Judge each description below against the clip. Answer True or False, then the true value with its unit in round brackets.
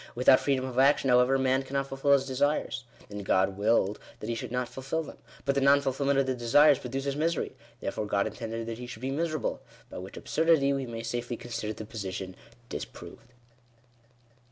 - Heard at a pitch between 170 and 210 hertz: False (130 Hz)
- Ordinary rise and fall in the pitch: True (3.1 semitones)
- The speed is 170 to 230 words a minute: True (195 wpm)